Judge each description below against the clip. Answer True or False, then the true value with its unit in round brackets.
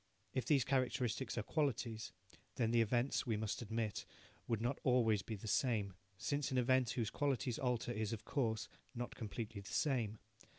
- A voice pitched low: True (120 Hz)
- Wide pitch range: False (2.7 semitones)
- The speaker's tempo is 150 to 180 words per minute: True (170 wpm)